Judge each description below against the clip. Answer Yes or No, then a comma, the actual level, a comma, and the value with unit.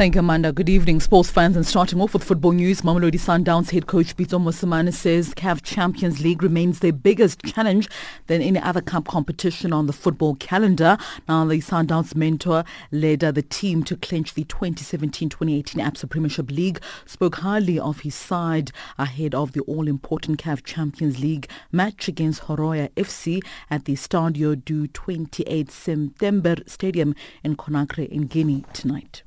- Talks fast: No, average, 160 wpm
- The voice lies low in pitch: No, medium, 165 Hz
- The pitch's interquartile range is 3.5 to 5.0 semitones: No, average, 2.9 semitones